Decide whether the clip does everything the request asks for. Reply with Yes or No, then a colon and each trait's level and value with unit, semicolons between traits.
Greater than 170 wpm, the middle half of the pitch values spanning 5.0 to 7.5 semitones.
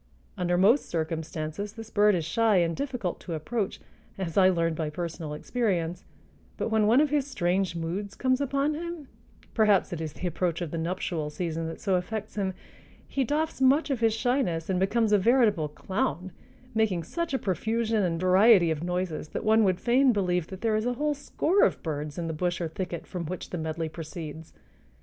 Yes: average, 190 wpm; average, 5.3 semitones